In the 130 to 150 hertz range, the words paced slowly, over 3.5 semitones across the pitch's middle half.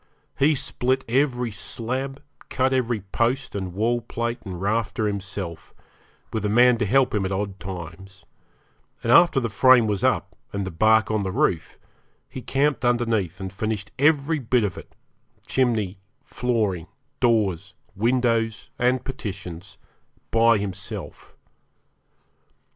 No: low, 110 Hz; slow, 130 wpm; average, 4.2 semitones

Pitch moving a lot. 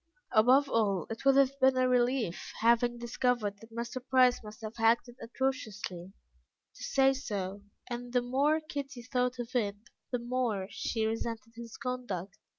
No: narrow, 2.6 semitones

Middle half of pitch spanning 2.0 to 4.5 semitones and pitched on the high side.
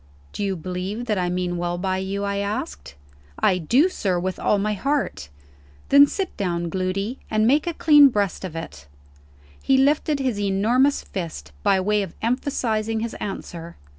No: average, 5.1 semitones; high, 200 Hz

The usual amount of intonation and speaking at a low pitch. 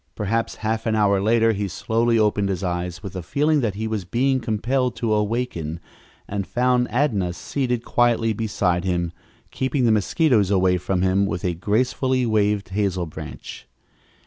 Yes: average, 4.1 semitones; low, 105 Hz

